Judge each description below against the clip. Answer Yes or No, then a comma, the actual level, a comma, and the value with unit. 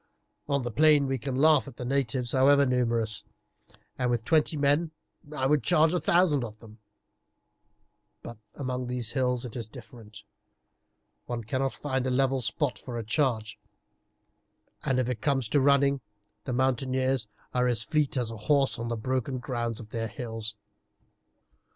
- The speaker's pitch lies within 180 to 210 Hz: No, low, 130 Hz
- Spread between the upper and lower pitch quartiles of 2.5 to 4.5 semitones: Yes, average, 3.0 semitones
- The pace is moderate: Yes, average, 165 wpm